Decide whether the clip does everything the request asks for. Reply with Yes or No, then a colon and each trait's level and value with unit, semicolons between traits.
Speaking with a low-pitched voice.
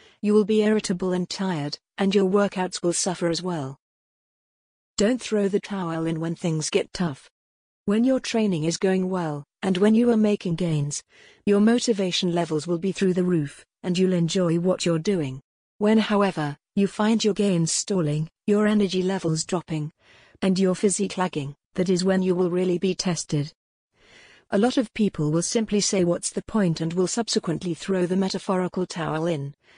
No: medium, 185 Hz